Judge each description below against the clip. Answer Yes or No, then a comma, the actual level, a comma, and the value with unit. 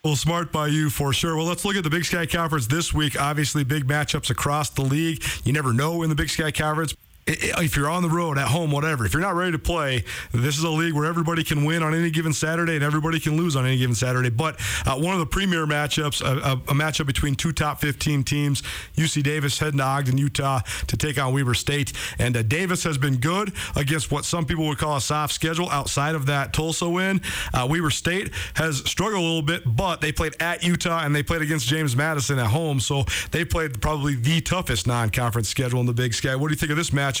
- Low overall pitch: No, medium, 150 Hz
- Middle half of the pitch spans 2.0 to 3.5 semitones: Yes, average, 3.0 semitones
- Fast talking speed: Yes, fast, 245 wpm